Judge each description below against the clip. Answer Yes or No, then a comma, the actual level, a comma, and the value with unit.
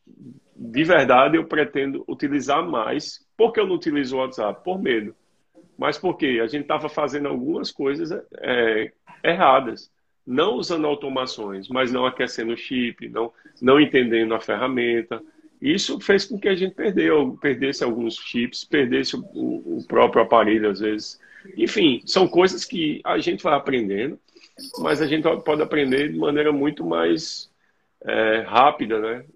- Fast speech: No, average, 150 wpm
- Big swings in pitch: Yes, wide, 8.8 semitones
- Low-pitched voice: No, medium, 145 Hz